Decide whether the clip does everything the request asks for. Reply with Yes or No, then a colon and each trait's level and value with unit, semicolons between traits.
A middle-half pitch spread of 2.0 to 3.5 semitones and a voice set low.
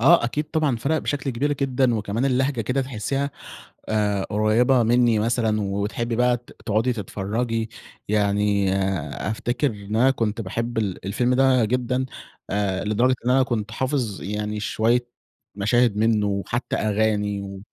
Yes: average, 3.2 semitones; low, 115 Hz